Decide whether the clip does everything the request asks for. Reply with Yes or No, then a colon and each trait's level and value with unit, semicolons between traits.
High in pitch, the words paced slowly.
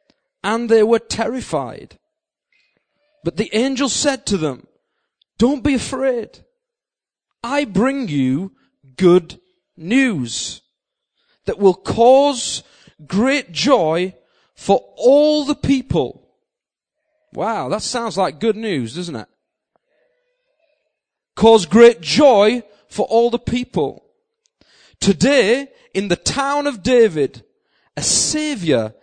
Yes: high, 245 Hz; slow, 105 wpm